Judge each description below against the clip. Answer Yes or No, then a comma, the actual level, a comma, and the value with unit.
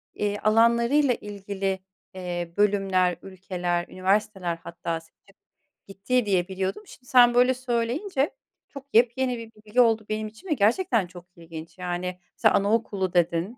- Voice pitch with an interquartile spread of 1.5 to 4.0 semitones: No, average, 4.5 semitones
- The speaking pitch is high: Yes, high, 205 Hz